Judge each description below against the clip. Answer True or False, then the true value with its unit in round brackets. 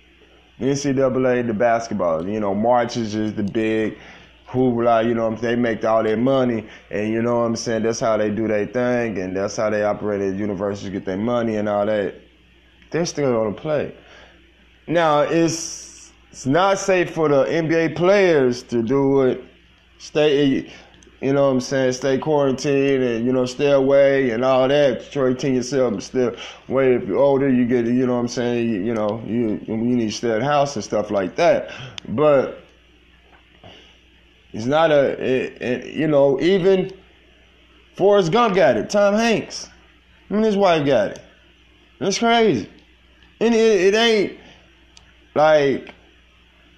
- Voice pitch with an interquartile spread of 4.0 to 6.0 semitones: True (5.0 semitones)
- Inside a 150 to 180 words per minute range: True (175 wpm)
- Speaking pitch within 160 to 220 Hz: False (125 Hz)